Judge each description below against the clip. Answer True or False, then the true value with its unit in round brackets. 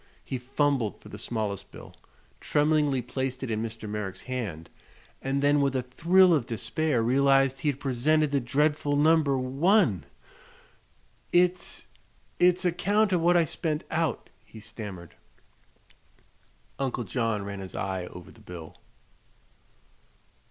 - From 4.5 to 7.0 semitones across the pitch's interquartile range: True (5.6 semitones)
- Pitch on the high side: False (135 Hz)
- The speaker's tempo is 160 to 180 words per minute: False (140 wpm)